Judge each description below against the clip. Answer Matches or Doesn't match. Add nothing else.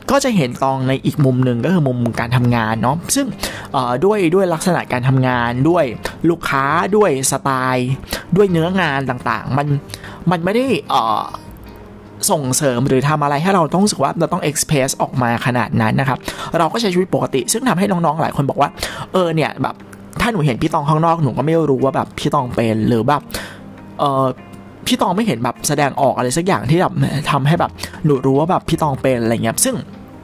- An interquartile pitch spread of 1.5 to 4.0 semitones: Doesn't match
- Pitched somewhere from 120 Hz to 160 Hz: Matches